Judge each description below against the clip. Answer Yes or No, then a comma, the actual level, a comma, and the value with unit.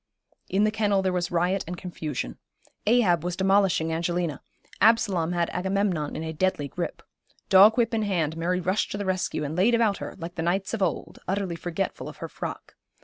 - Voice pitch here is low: No, medium, 180 Hz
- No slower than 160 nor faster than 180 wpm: No, average, 195 wpm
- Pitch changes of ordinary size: Yes, average, 3.0 semitones